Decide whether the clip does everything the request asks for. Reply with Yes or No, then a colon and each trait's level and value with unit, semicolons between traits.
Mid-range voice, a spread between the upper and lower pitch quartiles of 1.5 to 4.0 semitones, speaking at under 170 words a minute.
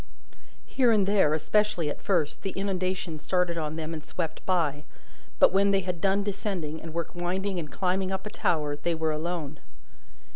No: medium, 175 Hz; average, 3.5 semitones; average, 180 wpm